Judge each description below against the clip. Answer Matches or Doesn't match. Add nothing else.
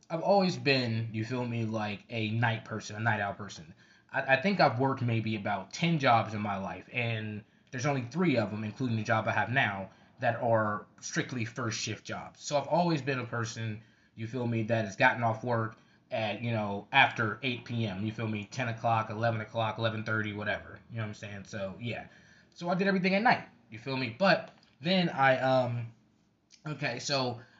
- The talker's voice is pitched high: Doesn't match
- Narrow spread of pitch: Doesn't match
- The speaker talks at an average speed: Doesn't match